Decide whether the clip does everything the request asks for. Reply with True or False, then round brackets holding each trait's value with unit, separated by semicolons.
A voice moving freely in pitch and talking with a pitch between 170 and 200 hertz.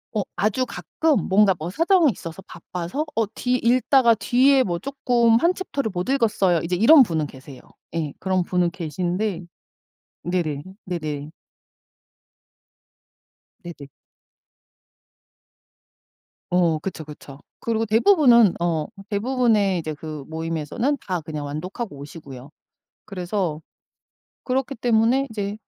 True (6.6 semitones; 190 Hz)